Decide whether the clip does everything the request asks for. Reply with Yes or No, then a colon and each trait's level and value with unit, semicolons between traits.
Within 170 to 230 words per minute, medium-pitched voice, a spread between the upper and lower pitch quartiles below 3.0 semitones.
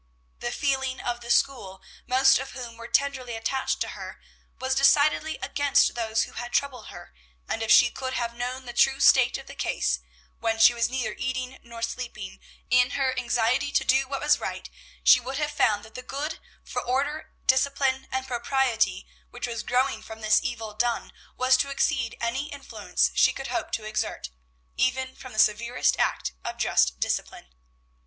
No: average, 180 wpm; very high, 250 Hz; narrow, 2.5 semitones